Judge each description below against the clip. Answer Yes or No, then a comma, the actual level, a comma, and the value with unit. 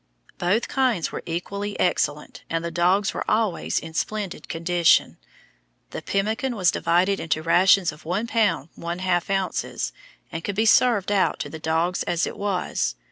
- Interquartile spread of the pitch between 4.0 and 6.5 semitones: No, average, 3.4 semitones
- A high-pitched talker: No, medium, 180 Hz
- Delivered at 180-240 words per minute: No, average, 160 wpm